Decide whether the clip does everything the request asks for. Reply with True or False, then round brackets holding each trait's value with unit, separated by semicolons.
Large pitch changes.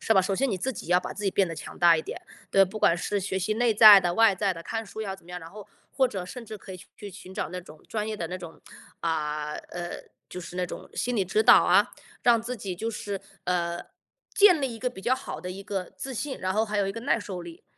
False (3.7 semitones)